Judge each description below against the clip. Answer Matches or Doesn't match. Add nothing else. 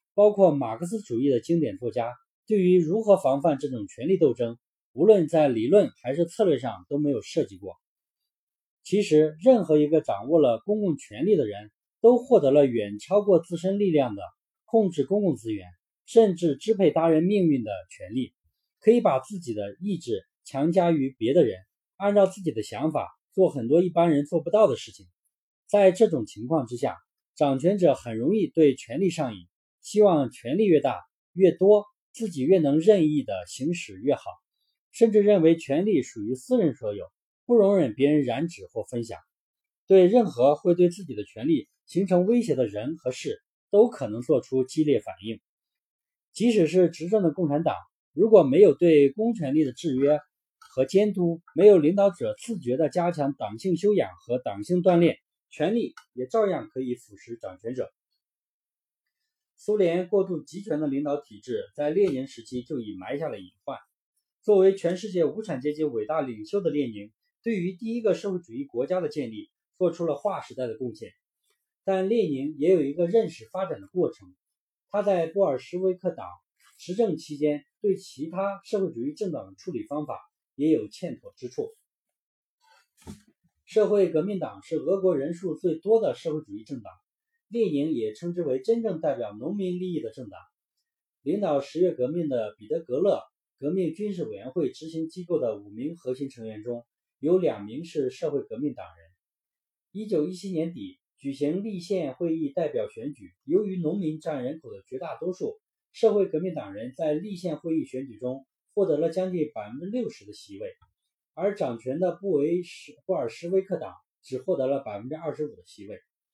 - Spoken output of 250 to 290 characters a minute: Matches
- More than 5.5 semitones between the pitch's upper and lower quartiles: Matches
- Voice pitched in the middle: Matches